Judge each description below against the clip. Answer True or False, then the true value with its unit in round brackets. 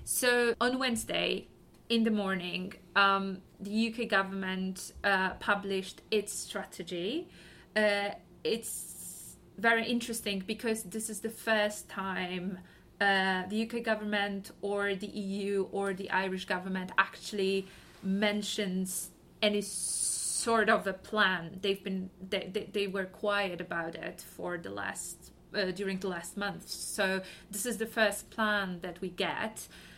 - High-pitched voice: True (200 Hz)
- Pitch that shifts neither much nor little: False (2.1 semitones)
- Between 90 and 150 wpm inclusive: True (135 wpm)